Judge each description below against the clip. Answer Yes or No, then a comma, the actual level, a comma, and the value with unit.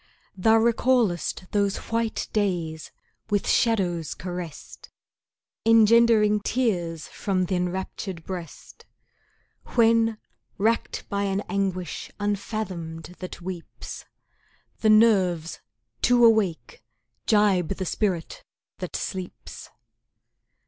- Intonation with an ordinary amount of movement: Yes, average, 3.8 semitones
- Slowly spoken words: Yes, slow, 90 wpm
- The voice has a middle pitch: No, high, 195 Hz